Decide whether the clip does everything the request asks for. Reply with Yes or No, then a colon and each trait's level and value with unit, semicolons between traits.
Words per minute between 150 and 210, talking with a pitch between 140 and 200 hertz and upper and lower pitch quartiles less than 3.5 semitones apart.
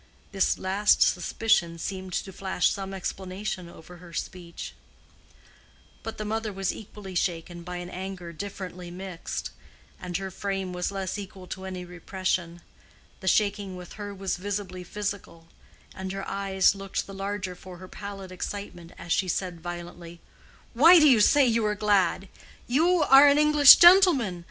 Yes: average, 155 wpm; high, 190 Hz; narrow, 2.4 semitones